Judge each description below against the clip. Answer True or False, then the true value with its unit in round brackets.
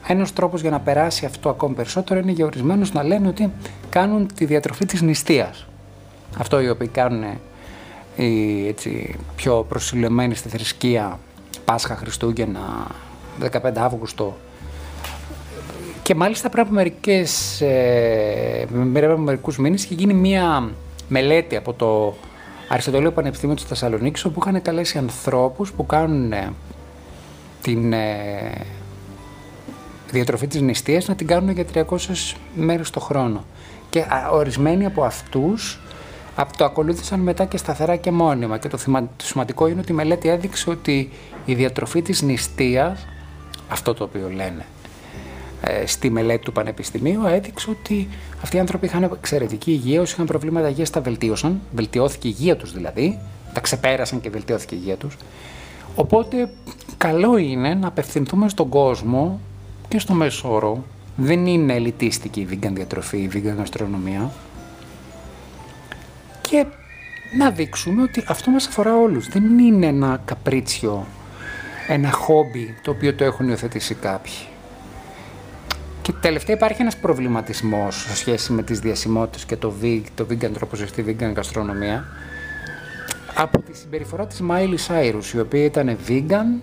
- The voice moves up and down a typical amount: False (7.6 semitones)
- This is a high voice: False (130 Hz)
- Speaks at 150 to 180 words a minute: False (135 wpm)